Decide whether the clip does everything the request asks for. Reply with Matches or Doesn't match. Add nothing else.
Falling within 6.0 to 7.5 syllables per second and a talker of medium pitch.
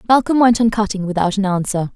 Doesn't match